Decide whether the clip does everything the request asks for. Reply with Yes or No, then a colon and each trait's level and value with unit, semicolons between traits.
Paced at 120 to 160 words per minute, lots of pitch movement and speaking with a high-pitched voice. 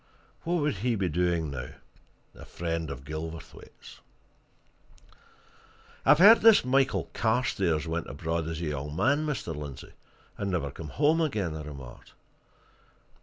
No: average, 145 wpm; wide, 8.9 semitones; very low, 85 Hz